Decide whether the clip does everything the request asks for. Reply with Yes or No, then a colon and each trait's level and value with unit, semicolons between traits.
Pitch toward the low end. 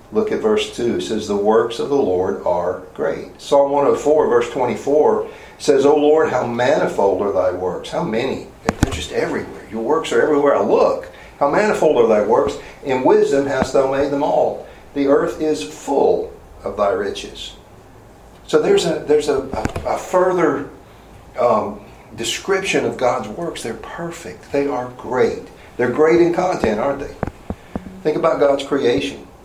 No: medium, 170 Hz